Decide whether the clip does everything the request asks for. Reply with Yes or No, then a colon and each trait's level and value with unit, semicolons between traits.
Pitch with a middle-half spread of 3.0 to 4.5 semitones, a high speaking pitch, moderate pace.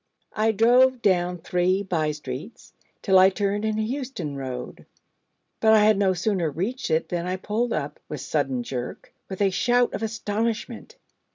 Yes: average, 4.1 semitones; high, 200 Hz; average, 165 wpm